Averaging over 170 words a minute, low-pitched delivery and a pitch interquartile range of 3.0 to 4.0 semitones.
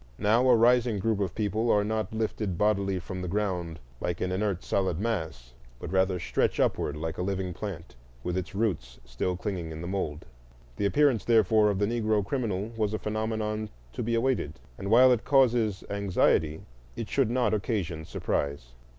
Yes: average, 180 wpm; low, 100 Hz; average, 3.6 semitones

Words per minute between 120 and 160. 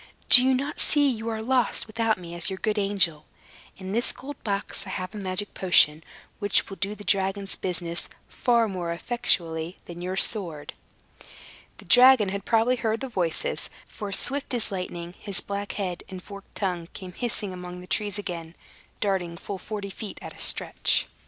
No: average, 180 wpm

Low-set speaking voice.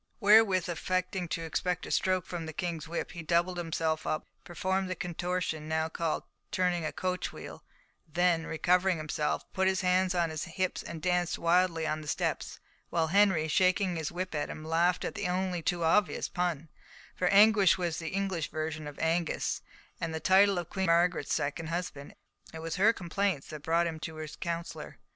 No: medium, 175 Hz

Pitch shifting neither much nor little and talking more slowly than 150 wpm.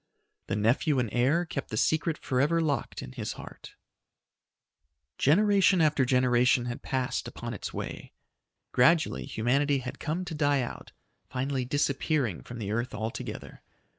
Yes: average, 3.9 semitones; average, 140 wpm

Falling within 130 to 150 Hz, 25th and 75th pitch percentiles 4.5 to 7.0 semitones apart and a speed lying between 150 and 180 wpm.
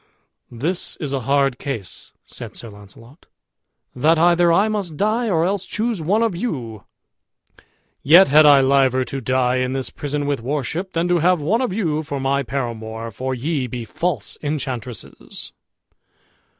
Yes: medium, 140 Hz; wide, 5.4 semitones; average, 160 wpm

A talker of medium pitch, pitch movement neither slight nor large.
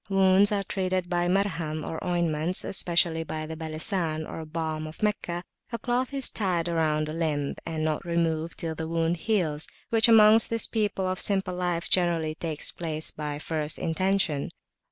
Yes: medium, 170 Hz; average, 3.3 semitones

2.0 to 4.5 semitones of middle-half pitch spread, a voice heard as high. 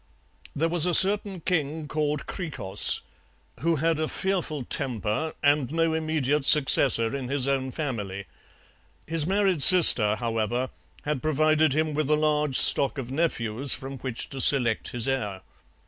No: average, 3.8 semitones; medium, 145 Hz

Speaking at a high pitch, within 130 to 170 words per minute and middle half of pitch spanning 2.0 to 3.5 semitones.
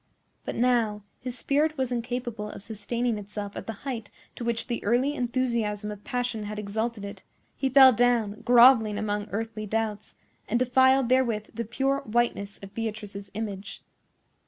Yes: high, 230 Hz; average, 155 wpm; average, 2.9 semitones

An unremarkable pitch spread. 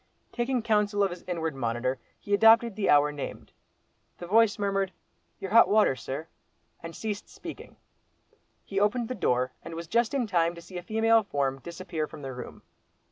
No: wide, 6.0 semitones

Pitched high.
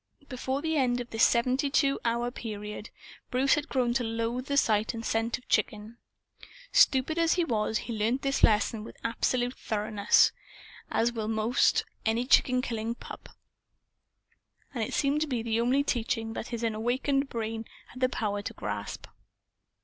Yes: high, 235 Hz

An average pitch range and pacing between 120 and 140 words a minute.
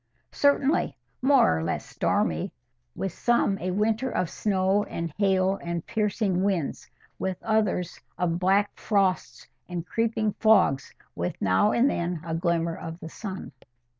Yes: average, 3.9 semitones; slow, 135 wpm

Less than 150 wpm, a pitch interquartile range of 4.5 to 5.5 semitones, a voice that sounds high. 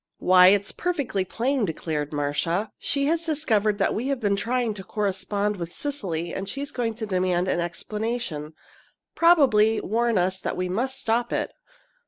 No: average, 165 wpm; average, 5.0 semitones; high, 210 Hz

